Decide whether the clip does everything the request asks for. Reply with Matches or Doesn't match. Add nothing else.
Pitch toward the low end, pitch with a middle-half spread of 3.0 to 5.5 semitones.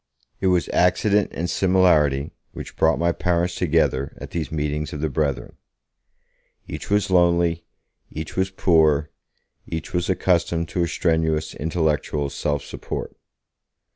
Doesn't match